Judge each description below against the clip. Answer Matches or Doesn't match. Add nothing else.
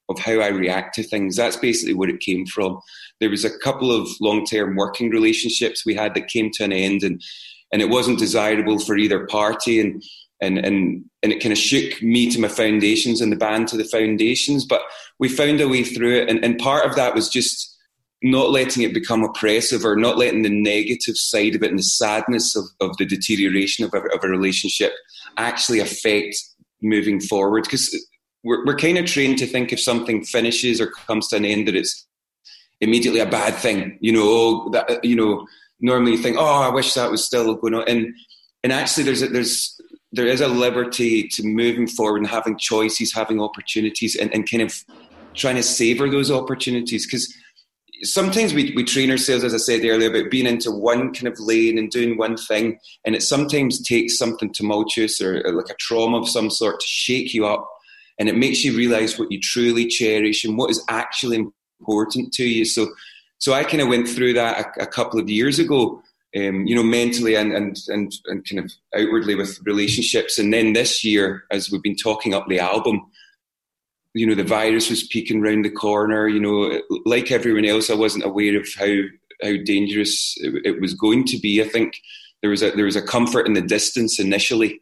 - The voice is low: Matches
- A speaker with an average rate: Doesn't match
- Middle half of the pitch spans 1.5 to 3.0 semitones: Matches